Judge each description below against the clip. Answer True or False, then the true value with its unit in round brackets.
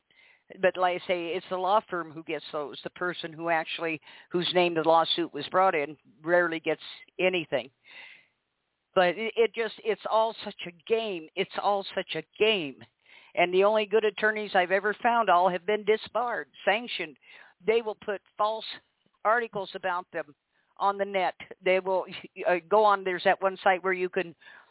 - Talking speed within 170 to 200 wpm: True (175 wpm)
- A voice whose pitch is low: False (185 Hz)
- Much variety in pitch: False (3.4 semitones)